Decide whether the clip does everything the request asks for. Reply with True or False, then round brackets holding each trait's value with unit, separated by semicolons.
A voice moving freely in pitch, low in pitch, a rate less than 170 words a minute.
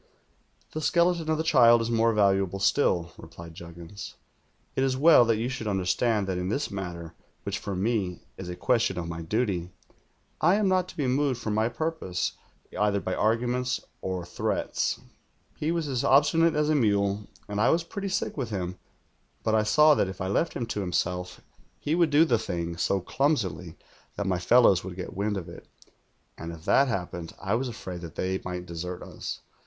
False (6.7 semitones; 105 Hz; 200 wpm)